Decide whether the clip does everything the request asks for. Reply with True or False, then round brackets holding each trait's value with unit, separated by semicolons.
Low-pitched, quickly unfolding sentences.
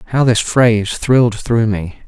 False (115 Hz; 175 wpm)